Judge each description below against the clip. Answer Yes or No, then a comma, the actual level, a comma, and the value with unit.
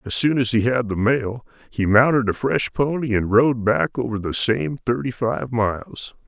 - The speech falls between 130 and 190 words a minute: No, average, 200 wpm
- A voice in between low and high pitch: No, low, 115 Hz